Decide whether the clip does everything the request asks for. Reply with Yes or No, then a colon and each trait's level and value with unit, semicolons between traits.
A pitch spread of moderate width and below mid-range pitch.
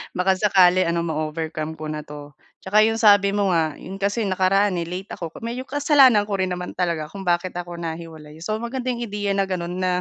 No: average, 3.3 semitones; medium, 185 Hz